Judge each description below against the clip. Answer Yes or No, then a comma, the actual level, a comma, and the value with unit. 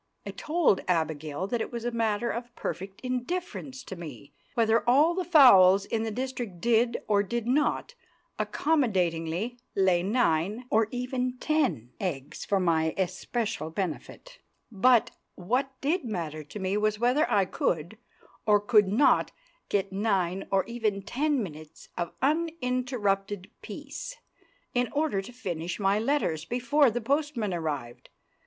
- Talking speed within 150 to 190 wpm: No, average, 140 wpm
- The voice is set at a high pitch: Yes, high, 215 Hz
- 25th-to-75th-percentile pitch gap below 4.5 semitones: No, average, 5.3 semitones